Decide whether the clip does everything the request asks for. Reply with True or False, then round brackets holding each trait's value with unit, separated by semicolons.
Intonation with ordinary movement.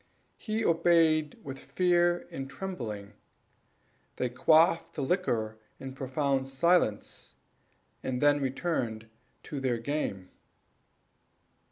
True (5.0 semitones)